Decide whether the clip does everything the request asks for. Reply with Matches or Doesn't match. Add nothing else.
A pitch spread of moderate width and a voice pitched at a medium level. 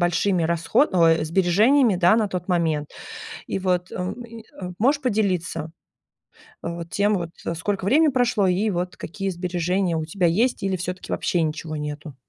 Matches